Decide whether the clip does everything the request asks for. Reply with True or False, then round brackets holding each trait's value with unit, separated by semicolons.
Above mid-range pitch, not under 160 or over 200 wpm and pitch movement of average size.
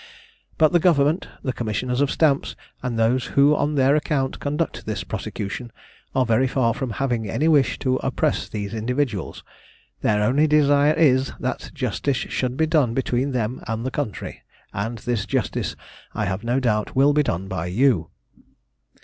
False (130 Hz; 165 wpm; 4.0 semitones)